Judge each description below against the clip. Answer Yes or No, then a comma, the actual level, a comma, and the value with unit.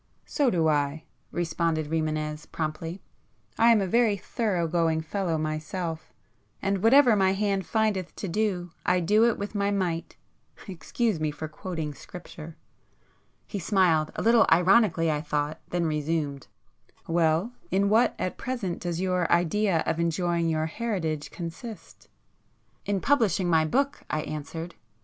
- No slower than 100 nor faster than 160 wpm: Yes, average, 145 wpm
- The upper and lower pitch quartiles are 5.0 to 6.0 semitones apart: No, average, 4.1 semitones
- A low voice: No, medium, 175 Hz